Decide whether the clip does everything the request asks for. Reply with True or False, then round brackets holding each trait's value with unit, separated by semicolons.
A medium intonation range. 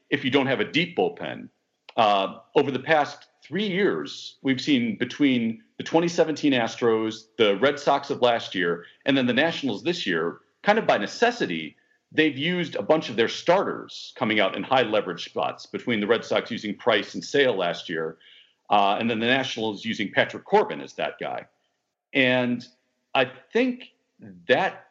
False (7.8 semitones)